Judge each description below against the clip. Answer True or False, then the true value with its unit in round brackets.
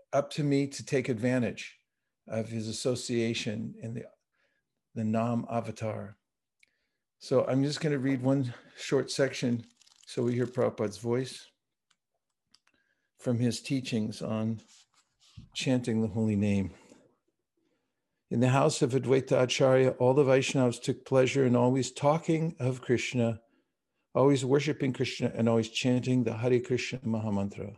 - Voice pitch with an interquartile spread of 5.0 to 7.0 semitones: False (2.7 semitones)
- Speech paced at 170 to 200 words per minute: False (135 wpm)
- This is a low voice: True (125 Hz)